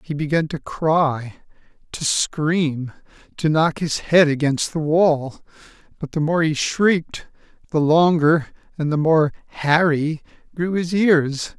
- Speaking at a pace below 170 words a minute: Yes, average, 140 wpm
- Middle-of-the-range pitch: Yes, medium, 155 Hz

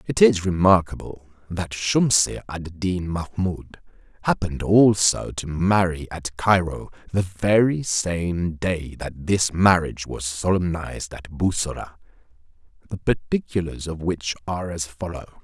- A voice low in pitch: Yes, very low, 90 Hz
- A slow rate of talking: Yes, slow, 125 wpm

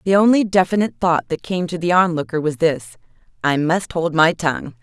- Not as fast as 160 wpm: No, average, 185 wpm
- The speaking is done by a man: No, female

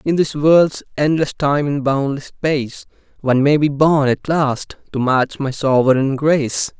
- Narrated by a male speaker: Yes, male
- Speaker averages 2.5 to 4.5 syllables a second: Yes, 4.3 syllables/s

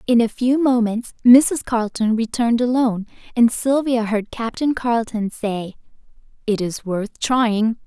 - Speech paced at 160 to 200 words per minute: No, slow, 135 wpm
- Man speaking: No, female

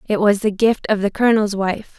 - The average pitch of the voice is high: Yes, high, 205 Hz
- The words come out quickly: Yes, fast, 240 wpm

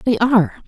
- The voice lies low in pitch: No, high, 220 Hz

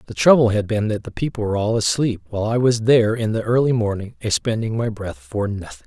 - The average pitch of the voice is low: Yes, low, 110 Hz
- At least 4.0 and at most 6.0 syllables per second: No, 6.2 syllables/s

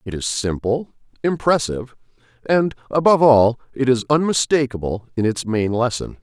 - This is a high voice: No, low, 125 Hz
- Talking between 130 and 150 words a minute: Yes, slow, 135 wpm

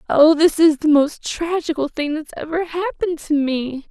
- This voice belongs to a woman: Yes, female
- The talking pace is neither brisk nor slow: Yes, average, 185 wpm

